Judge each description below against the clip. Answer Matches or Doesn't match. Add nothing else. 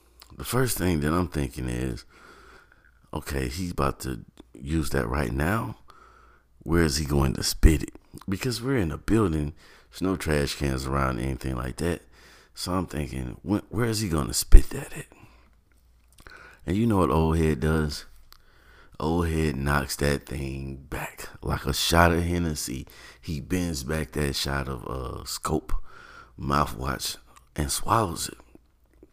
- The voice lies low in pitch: Matches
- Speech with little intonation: Doesn't match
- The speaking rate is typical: Matches